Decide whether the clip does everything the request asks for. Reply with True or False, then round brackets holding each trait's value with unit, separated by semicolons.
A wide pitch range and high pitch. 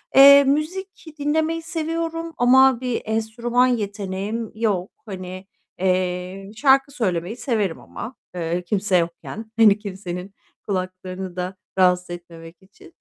True (6.3 semitones; 205 Hz)